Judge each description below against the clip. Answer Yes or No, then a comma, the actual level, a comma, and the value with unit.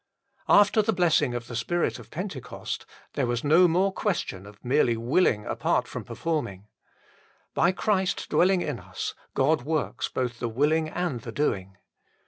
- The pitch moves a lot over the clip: Yes, wide, 7.0 semitones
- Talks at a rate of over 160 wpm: No, average, 155 wpm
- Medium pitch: Yes, medium, 150 Hz